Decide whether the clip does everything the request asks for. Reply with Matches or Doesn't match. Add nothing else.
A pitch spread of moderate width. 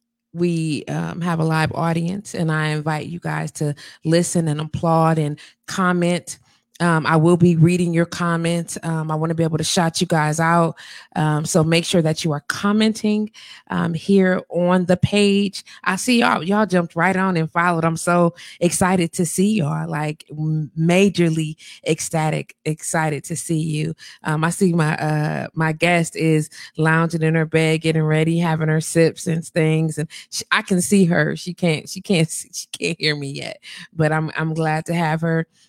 Doesn't match